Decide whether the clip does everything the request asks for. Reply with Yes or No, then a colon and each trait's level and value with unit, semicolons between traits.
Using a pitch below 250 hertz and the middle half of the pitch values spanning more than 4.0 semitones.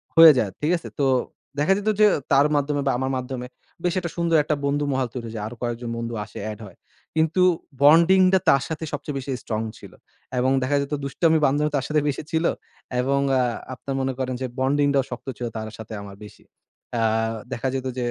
No: medium, 140 Hz; average, 3.7 semitones